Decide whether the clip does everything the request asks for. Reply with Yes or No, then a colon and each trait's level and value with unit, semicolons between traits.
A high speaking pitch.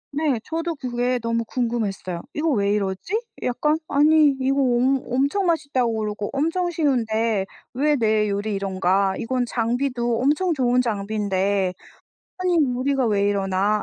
Yes: high, 240 Hz